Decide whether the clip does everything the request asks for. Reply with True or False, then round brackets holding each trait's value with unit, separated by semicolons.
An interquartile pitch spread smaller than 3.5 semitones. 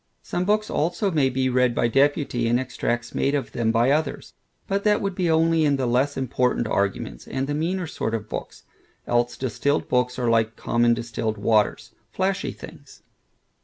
False (5.1 semitones)